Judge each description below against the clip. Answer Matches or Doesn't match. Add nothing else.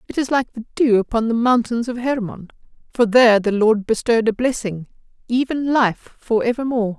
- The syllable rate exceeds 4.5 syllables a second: Matches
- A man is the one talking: Doesn't match